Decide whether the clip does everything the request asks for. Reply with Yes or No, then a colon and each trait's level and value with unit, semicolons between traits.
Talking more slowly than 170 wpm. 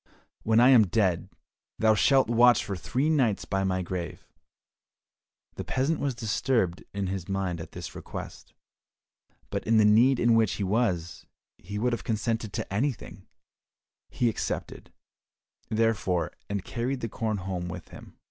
Yes: average, 155 wpm